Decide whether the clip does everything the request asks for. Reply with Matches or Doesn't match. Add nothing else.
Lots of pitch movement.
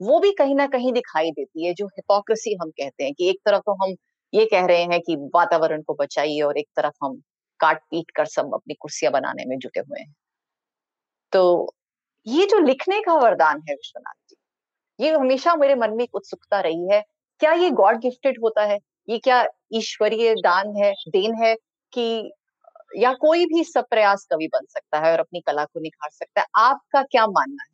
Matches